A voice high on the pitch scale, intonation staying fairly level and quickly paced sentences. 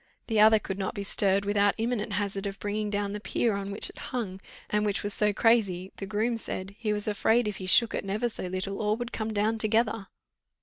Yes: high, 210 Hz; narrow, 1.9 semitones; fast, 230 wpm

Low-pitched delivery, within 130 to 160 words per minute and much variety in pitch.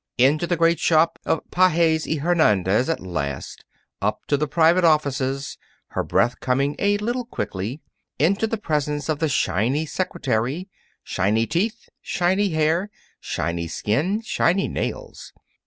No: medium, 155 Hz; average, 140 wpm; wide, 5.8 semitones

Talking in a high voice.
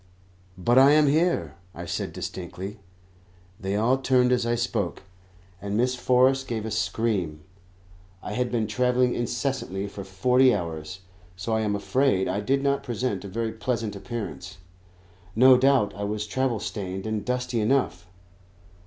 No: low, 115 Hz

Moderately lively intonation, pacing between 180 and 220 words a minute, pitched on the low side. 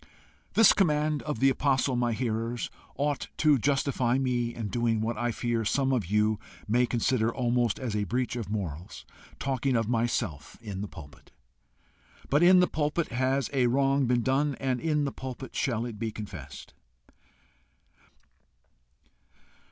No: average, 3.4 semitones; average, 150 wpm; low, 120 Hz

